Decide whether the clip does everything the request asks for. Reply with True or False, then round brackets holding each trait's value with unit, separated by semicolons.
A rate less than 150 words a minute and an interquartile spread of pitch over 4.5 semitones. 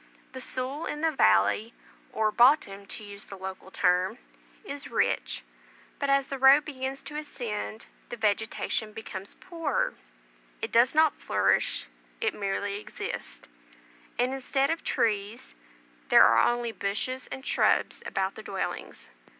True (140 wpm; 5.4 semitones)